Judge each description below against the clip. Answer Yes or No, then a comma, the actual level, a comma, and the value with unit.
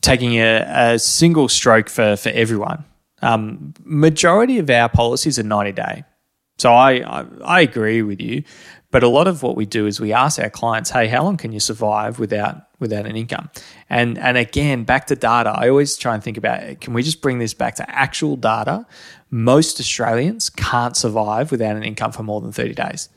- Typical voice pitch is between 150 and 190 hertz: No, low, 115 Hz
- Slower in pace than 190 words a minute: No, average, 200 wpm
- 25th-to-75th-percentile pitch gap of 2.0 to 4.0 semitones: Yes, average, 3.3 semitones